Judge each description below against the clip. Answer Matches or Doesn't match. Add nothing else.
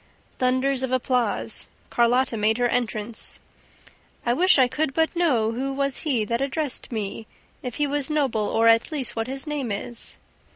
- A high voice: Matches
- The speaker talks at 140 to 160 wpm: Doesn't match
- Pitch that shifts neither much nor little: Matches